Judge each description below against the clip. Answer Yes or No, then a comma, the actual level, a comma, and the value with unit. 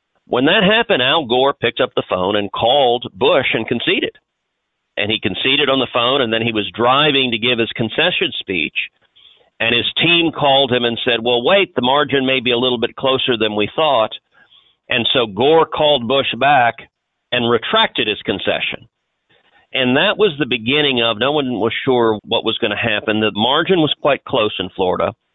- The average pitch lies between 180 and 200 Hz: No, low, 125 Hz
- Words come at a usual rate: Yes, average, 195 wpm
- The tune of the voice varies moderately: Yes, average, 3.8 semitones